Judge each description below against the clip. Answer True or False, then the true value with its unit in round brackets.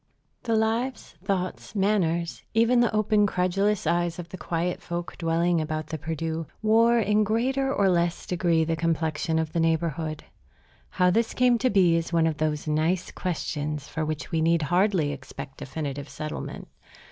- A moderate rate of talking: True (165 wpm)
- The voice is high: False (170 Hz)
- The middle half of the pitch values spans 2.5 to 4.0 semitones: False (4.4 semitones)